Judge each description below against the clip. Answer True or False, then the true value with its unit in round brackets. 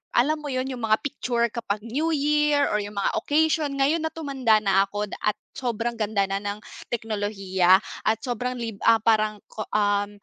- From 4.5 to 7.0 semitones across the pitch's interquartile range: True (5.0 semitones)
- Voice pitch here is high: True (225 Hz)